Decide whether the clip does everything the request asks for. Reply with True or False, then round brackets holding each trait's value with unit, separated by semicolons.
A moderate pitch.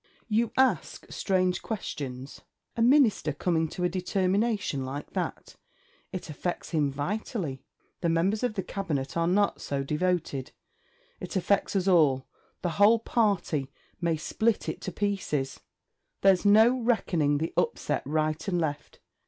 True (180 Hz)